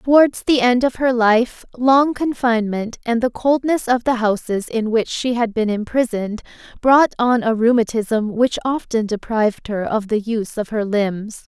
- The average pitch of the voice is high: Yes, high, 230 Hz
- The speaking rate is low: No, average, 175 wpm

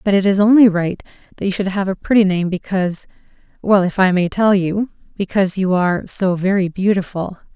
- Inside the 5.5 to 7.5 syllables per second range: Yes, 5.7 syllables/s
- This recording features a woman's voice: Yes, female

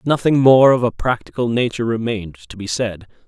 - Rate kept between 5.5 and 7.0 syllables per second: Yes, 5.9 syllables/s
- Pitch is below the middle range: Yes, low, 115 Hz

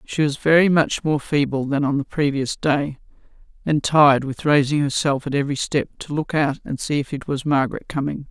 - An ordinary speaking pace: No, fast, 210 wpm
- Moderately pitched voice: Yes, medium, 145 Hz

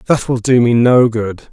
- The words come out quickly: Yes, fast, 235 wpm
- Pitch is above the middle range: No, low, 120 Hz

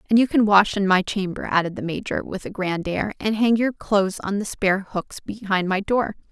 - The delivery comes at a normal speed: No, fast, 235 wpm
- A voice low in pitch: No, high, 200 Hz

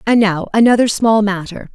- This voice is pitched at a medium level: No, high, 210 Hz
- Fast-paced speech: No, average, 170 wpm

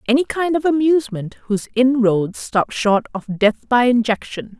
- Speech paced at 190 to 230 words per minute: No, average, 155 wpm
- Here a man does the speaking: No, female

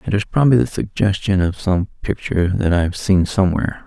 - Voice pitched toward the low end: Yes, very low, 95 Hz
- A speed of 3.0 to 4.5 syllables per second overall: No, 6.2 syllables/s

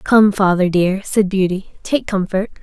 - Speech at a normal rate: Yes, average, 160 wpm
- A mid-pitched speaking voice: No, high, 195 Hz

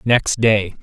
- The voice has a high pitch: No, low, 110 Hz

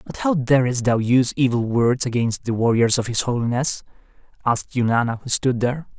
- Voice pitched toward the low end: Yes, low, 125 Hz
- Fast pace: No, average, 180 wpm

